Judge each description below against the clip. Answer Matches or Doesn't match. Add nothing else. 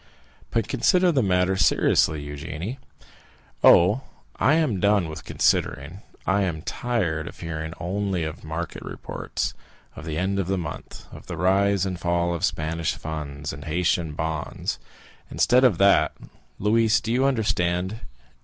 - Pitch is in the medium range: Doesn't match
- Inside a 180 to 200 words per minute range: Doesn't match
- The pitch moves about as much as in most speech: Matches